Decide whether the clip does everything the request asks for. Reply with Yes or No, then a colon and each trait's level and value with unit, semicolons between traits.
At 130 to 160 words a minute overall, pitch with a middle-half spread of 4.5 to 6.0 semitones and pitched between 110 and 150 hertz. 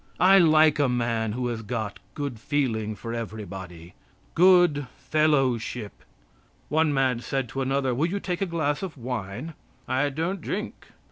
Yes: average, 150 wpm; average, 5.2 semitones; low, 135 Hz